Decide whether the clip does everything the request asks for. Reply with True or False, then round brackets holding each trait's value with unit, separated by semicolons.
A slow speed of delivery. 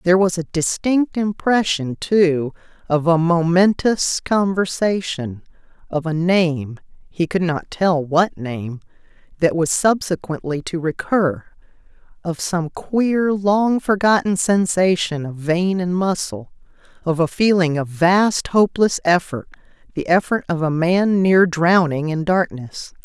True (125 wpm)